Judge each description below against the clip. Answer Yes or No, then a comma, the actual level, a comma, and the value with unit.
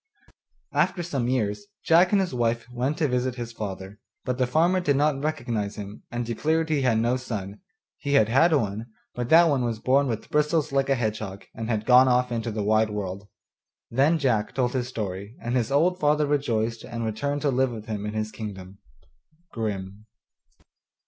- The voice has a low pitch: Yes, low, 120 Hz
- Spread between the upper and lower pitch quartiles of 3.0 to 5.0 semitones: Yes, average, 4.7 semitones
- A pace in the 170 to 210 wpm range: Yes, average, 190 wpm